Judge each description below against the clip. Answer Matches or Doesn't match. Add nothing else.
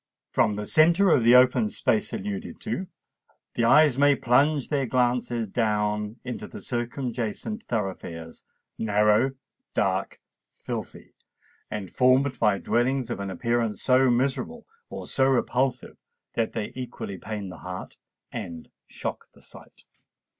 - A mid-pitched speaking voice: Doesn't match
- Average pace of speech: Doesn't match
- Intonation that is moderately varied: Matches